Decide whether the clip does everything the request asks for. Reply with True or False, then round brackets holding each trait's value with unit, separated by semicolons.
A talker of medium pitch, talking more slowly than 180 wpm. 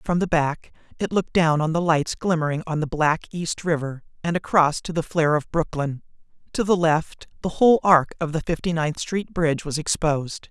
False (160 Hz; 205 wpm)